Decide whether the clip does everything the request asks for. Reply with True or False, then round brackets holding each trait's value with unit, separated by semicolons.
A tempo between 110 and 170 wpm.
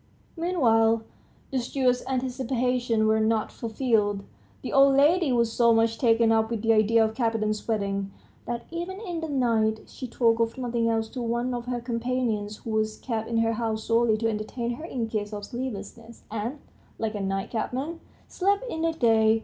False (180 wpm)